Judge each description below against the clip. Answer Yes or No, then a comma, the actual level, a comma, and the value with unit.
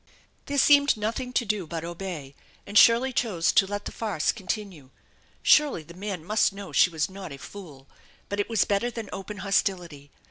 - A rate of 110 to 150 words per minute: No, average, 185 wpm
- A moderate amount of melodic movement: Yes, average, 4.3 semitones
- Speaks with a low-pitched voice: No, high, 200 Hz